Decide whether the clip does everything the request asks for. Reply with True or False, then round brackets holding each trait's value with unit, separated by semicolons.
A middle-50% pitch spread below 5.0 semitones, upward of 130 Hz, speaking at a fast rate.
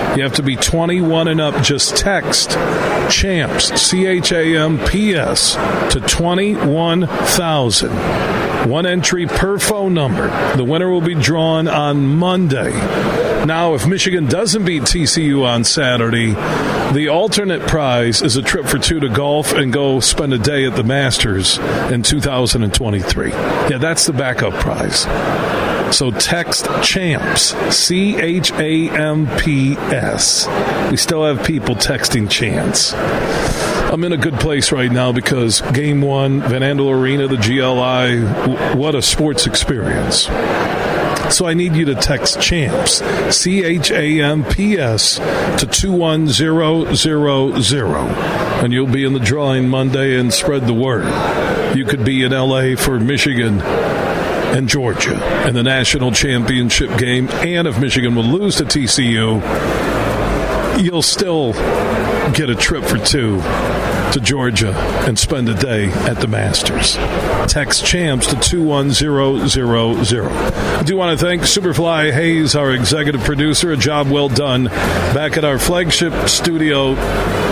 False (4.2 semitones; 140 Hz; 140 wpm)